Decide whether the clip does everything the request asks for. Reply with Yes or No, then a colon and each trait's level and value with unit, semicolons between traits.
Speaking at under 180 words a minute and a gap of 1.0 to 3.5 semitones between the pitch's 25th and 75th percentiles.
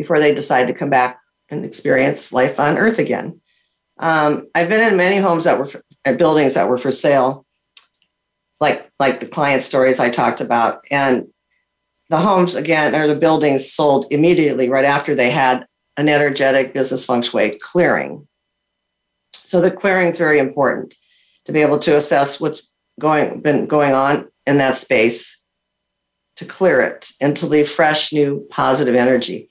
Yes: average, 170 wpm; average, 2.8 semitones